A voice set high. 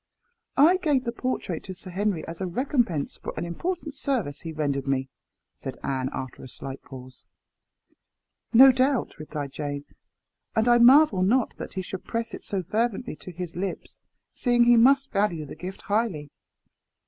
Yes: high, 195 Hz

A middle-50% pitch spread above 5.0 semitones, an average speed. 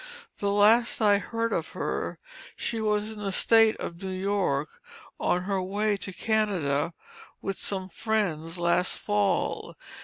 No: average, 3.0 semitones; average, 145 wpm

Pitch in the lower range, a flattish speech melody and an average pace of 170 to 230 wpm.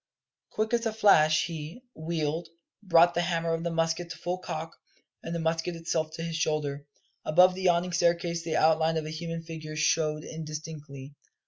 No: medium, 165 Hz; narrow, 1.6 semitones; average, 180 wpm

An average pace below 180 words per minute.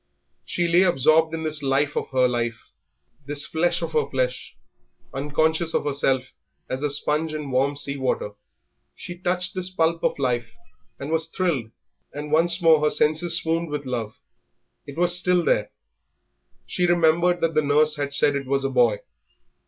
Yes: average, 170 wpm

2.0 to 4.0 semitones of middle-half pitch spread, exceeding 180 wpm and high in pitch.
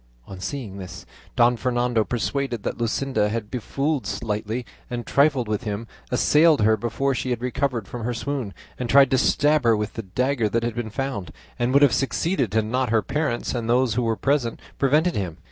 No: average, 3.6 semitones; average, 195 wpm; low, 120 Hz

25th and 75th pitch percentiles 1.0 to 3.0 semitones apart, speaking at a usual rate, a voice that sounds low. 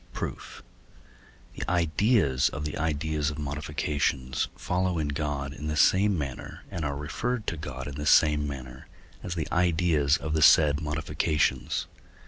Yes: narrow, 2.4 semitones; average, 150 wpm; very low, 75 Hz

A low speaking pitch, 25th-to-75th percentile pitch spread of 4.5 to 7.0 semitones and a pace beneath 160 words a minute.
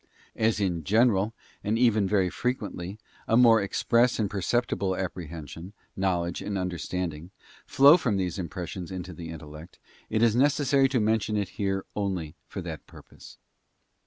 No: very low, 95 Hz; average, 4.1 semitones; average, 145 wpm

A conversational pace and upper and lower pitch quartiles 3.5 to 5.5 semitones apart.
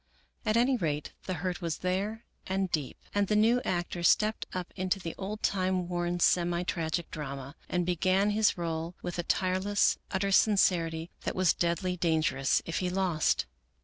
No: average, 170 wpm; narrow, 2.4 semitones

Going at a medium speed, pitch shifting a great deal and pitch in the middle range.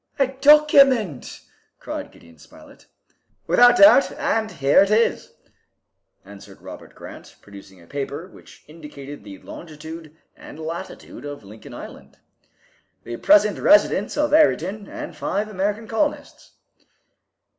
No: slow, 120 wpm; wide, 8.7 semitones; medium, 175 Hz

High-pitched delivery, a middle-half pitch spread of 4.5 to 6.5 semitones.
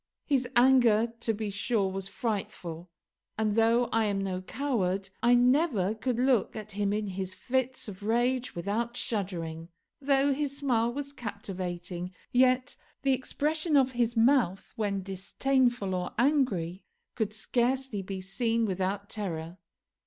Yes: high, 225 Hz; average, 4.8 semitones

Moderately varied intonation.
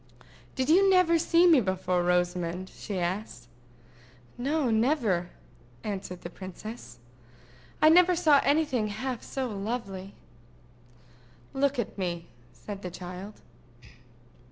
No: wide, 7.5 semitones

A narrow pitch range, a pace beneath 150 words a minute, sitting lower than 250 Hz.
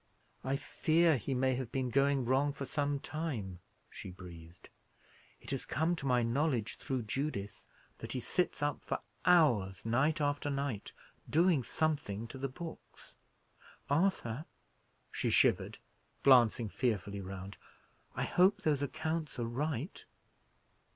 No: average, 4.8 semitones; slow, 135 wpm; low, 135 Hz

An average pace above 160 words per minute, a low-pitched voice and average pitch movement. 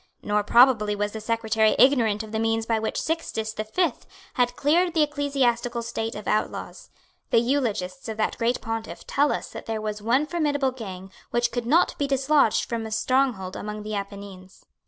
No: average, 185 wpm; high, 230 Hz; average, 4.0 semitones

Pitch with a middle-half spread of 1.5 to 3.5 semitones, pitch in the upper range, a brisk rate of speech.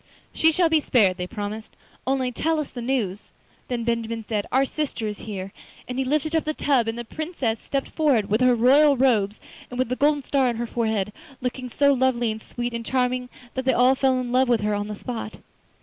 Yes: average, 3.2 semitones; very high, 250 Hz; fast, 225 wpm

